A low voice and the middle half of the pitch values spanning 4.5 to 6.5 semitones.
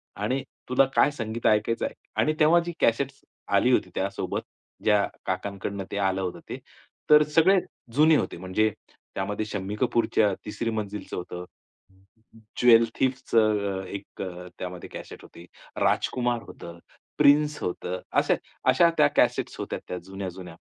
Yes: low, 105 Hz; average, 5.1 semitones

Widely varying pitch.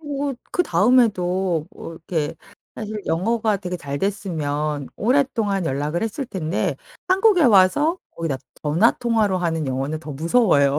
Yes: wide, 6.9 semitones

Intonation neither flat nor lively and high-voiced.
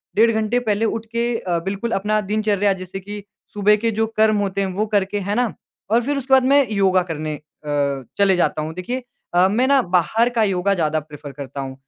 Yes: average, 3.5 semitones; high, 205 Hz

